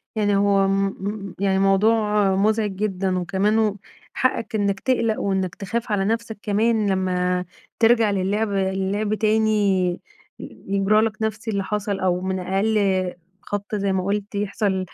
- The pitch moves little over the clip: Yes, narrow, 2.0 semitones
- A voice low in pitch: No, high, 200 Hz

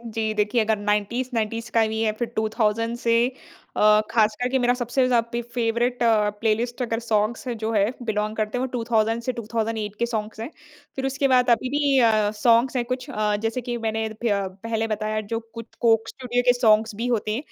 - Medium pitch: No, high, 230 Hz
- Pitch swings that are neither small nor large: No, narrow, 2.1 semitones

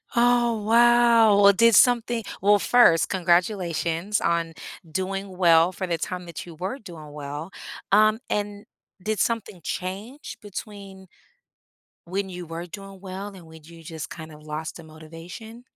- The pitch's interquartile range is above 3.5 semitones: Yes, average, 4.2 semitones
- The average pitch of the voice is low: No, high, 190 Hz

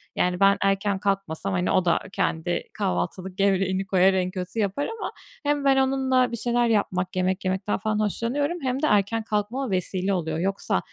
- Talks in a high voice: Yes, high, 195 Hz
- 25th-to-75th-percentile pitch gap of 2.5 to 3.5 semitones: No, average, 4.0 semitones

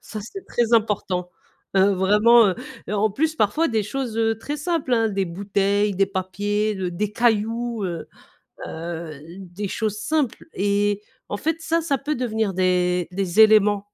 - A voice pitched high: Yes, high, 210 Hz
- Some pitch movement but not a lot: Yes, average, 3.4 semitones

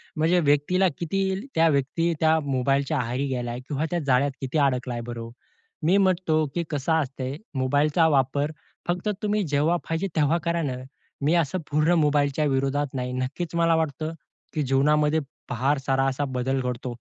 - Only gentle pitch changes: No, average, 3.5 semitones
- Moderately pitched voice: Yes, medium, 145 Hz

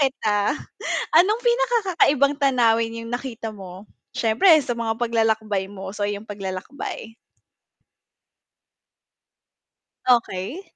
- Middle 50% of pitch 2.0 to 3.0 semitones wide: No, average, 5.2 semitones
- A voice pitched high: Yes, high, 230 Hz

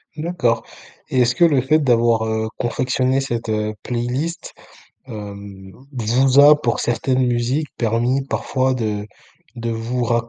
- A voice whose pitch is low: Yes, low, 120 Hz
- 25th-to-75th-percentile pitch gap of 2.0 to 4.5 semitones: Yes, average, 2.7 semitones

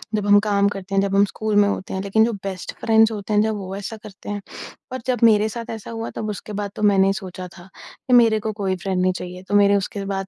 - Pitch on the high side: Yes, high, 205 Hz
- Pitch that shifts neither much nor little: No, narrow, 1.9 semitones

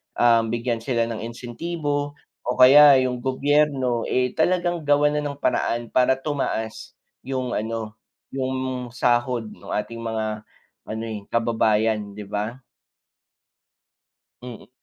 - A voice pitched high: No, low, 125 Hz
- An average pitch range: Yes, average, 3.2 semitones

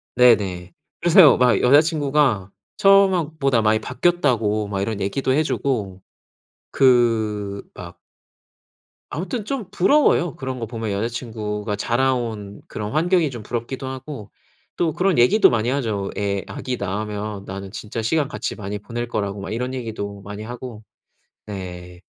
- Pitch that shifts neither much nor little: Yes, average, 5.0 semitones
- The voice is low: Yes, low, 115 Hz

